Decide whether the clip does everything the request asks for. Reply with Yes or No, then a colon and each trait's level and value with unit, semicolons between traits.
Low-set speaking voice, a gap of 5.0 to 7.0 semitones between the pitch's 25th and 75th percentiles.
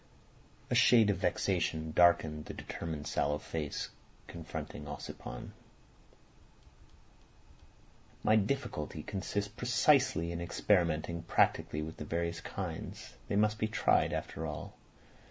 Yes: very low, 85 Hz; average, 5.3 semitones